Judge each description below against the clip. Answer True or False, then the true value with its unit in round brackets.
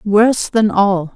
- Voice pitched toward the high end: True (205 Hz)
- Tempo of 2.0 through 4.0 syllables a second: True (3.6 syllables/s)